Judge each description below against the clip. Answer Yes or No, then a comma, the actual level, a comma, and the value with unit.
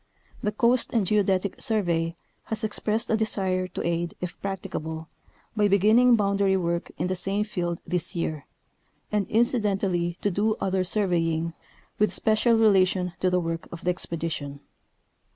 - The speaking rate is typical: Yes, average, 150 wpm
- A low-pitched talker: No, high, 190 Hz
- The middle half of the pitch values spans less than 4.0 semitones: Yes, average, 3.5 semitones